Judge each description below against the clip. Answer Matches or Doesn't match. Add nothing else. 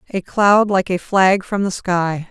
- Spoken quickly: Matches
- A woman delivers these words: Matches